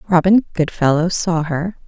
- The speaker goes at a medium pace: No, slow, 130 wpm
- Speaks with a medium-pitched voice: Yes, medium, 170 Hz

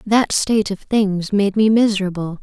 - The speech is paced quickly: No, average, 175 wpm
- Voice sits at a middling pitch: No, high, 205 Hz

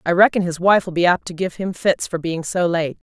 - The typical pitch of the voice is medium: Yes, medium, 175 Hz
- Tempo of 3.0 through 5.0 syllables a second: No, 5.5 syllables/s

